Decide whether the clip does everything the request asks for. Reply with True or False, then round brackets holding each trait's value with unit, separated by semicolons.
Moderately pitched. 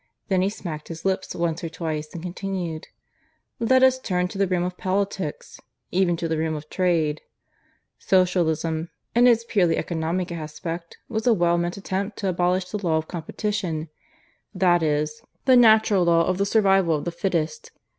True (180 Hz)